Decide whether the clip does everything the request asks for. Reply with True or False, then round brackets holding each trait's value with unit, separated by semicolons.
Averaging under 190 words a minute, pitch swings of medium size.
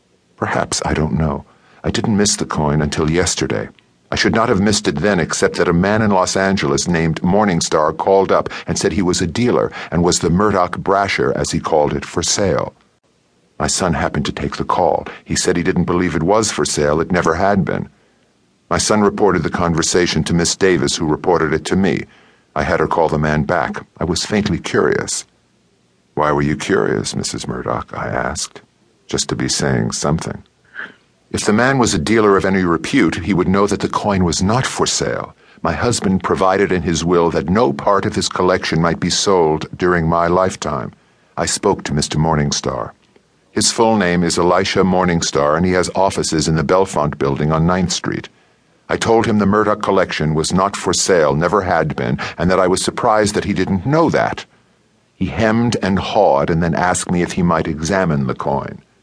False (200 wpm; 3.5 semitones)